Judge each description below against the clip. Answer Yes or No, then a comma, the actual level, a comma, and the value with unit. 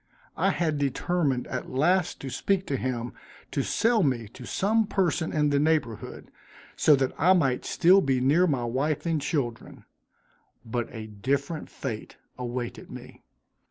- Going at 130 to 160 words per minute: Yes, average, 155 wpm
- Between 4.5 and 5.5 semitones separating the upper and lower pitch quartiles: Yes, average, 5.1 semitones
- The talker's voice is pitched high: No, medium, 140 Hz